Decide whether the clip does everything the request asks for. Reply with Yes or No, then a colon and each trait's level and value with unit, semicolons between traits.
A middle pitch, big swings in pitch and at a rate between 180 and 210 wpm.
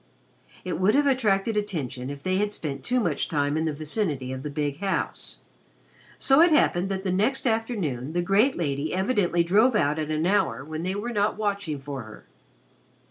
Yes: medium, 180 Hz; wide, 6.0 semitones; average, 190 wpm